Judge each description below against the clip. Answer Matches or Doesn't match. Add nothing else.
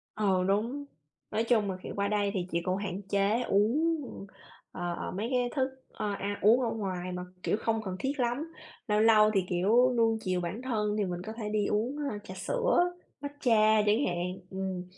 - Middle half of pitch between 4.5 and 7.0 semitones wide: Doesn't match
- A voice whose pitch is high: Matches